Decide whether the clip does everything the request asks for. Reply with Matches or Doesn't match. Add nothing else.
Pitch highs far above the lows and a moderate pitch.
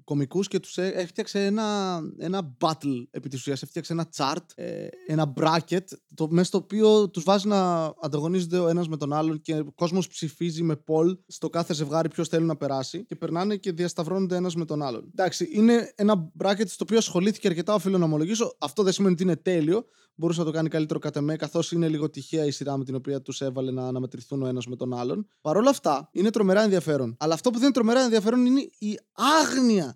Doesn't match